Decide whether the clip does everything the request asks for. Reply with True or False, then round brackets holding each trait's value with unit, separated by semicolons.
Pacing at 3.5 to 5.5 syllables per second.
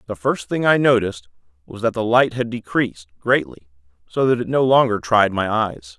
True (5.2 syllables/s)